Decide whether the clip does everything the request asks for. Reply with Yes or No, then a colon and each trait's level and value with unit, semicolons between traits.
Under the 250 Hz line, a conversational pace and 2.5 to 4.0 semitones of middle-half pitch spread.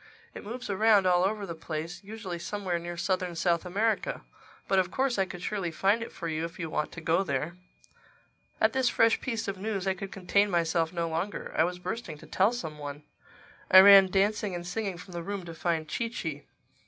No: medium, 185 Hz; fast, 210 wpm; average, 3.3 semitones